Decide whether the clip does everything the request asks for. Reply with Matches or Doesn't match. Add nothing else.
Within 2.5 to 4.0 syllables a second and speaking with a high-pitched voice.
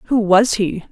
Matches